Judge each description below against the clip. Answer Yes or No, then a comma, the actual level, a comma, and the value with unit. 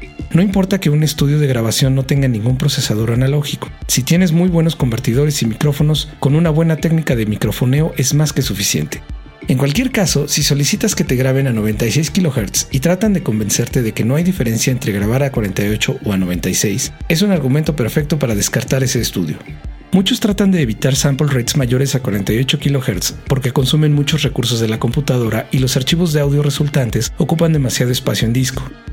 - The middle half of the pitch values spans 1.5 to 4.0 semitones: No, average, 4.4 semitones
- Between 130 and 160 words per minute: No, fast, 190 wpm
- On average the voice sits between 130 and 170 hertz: Yes, medium, 140 Hz